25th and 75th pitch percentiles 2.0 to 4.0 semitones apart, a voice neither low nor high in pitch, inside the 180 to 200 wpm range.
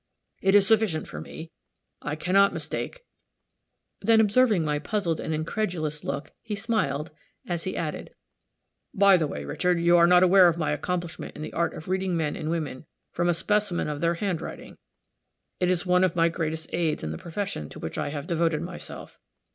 Yes: average, 3.3 semitones; medium, 170 Hz; average, 190 wpm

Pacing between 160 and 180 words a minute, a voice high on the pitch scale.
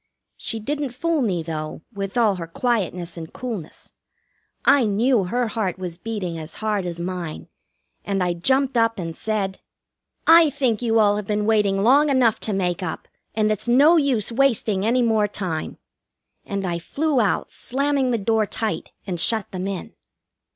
Yes: average, 170 wpm; high, 215 Hz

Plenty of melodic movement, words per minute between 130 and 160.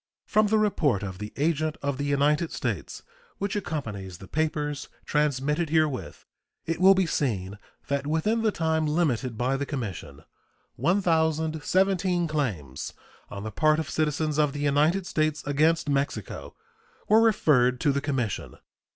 No: average, 3.3 semitones; average, 145 wpm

